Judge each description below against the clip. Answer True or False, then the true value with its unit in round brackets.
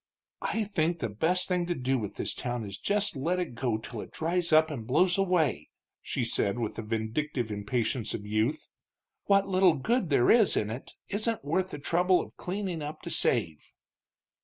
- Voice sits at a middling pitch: True (150 Hz)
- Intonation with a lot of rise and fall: True (7.9 semitones)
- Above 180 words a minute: True (190 wpm)